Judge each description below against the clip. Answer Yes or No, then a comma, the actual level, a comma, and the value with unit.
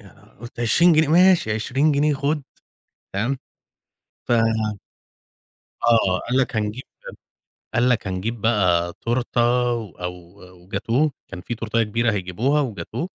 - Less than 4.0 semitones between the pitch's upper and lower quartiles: No, average, 4.8 semitones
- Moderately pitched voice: No, low, 120 Hz